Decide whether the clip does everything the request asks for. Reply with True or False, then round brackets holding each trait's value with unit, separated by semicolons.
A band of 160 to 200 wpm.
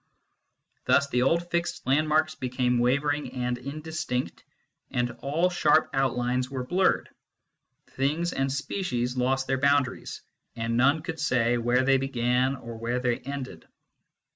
False (135 wpm)